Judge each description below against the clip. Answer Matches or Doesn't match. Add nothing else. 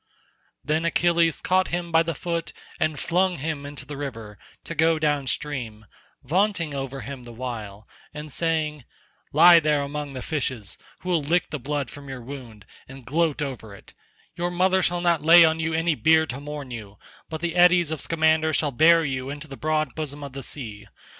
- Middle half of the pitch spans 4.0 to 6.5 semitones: Doesn't match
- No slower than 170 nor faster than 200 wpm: Matches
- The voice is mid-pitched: Matches